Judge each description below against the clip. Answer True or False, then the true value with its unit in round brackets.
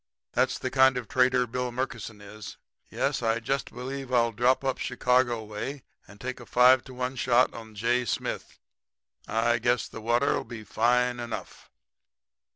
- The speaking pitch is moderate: False (120 Hz)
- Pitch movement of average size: False (1.9 semitones)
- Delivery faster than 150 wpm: True (160 wpm)